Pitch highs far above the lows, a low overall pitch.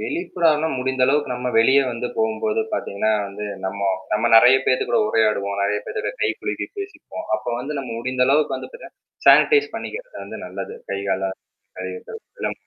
Yes: wide, 7.3 semitones; low, 125 Hz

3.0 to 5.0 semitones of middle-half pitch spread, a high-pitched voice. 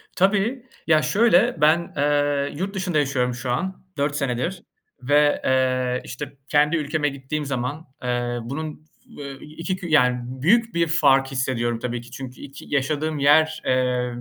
No: average, 3.7 semitones; medium, 145 Hz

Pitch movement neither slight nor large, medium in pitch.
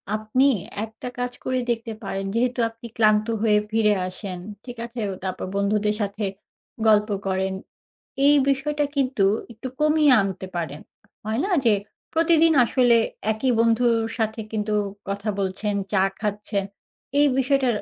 No: average, 3.7 semitones; high, 220 Hz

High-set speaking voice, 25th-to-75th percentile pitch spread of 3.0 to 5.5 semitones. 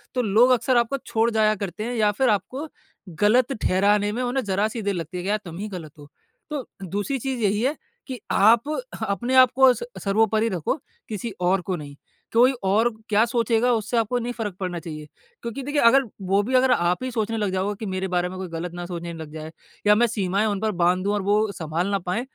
Yes: high, 210 Hz; average, 4.3 semitones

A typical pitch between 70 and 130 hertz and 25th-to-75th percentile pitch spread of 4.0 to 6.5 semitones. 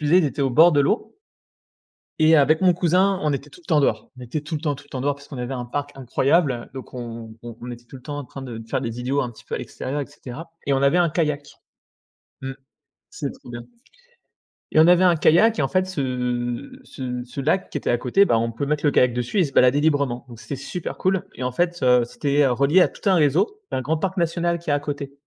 No: medium, 140 Hz; average, 4.4 semitones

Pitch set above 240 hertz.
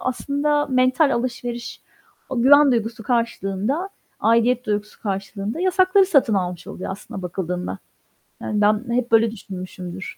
No: high, 230 Hz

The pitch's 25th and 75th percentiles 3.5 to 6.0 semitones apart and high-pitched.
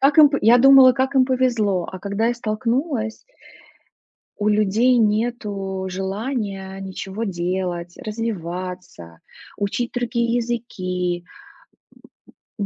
Yes: average, 4.2 semitones; high, 215 Hz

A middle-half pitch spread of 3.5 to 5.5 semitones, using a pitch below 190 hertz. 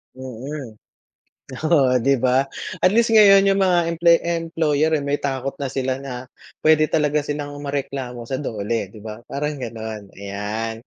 Yes: average, 4.3 semitones; medium, 140 Hz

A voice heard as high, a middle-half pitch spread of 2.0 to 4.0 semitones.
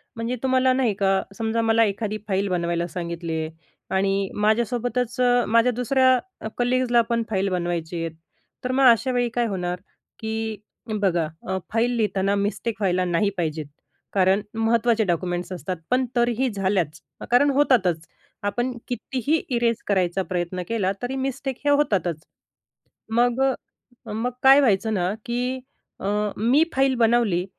No: high, 220 Hz; average, 4.7 semitones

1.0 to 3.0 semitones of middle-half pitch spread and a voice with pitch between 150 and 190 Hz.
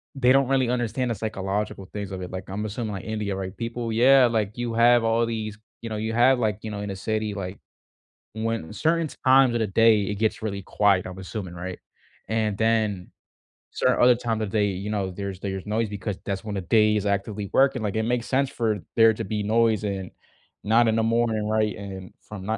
No: narrow, 2.5 semitones; low, 110 Hz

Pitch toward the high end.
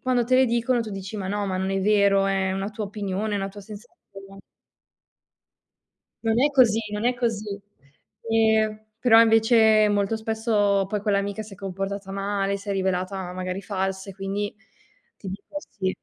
Yes: high, 205 Hz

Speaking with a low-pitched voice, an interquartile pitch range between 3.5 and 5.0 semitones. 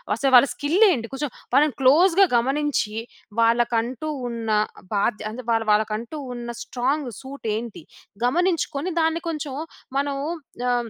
No: very high, 260 Hz; average, 4.2 semitones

